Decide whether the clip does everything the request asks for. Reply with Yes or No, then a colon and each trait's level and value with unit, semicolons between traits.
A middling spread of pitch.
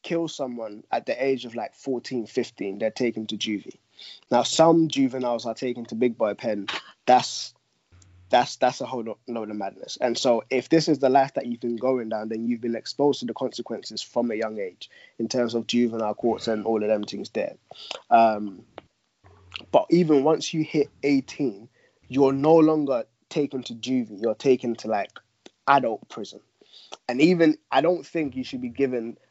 Yes: average, 3.6 semitones